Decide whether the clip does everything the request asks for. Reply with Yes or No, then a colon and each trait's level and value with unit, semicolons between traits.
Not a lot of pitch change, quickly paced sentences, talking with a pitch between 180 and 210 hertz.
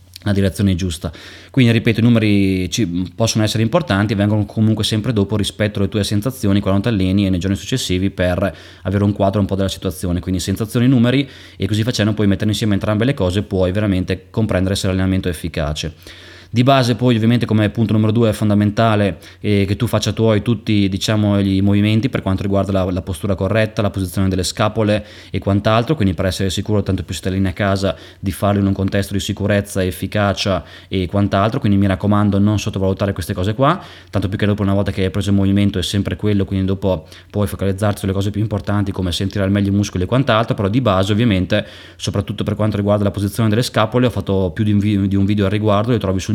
No: narrow, 2.0 semitones; fast, 215 wpm; low, 100 Hz